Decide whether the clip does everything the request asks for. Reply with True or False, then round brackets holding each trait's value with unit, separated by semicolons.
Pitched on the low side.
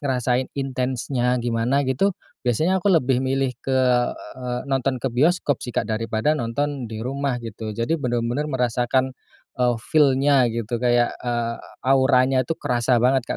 True (125 Hz)